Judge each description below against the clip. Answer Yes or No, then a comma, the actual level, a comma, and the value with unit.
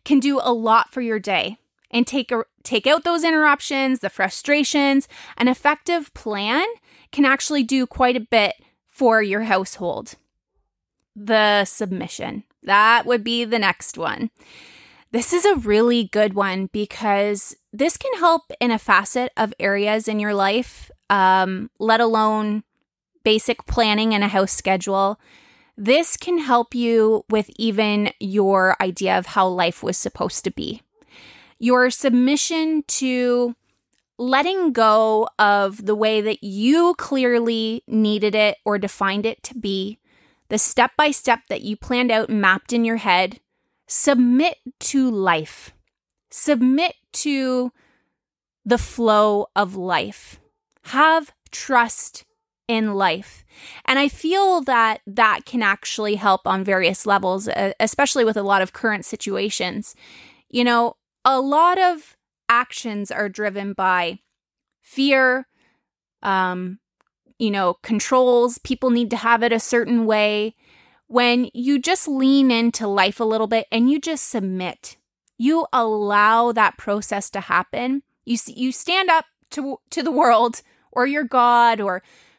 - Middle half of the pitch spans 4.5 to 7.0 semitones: No, average, 4.1 semitones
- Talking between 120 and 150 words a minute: Yes, average, 140 wpm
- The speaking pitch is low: No, high, 235 Hz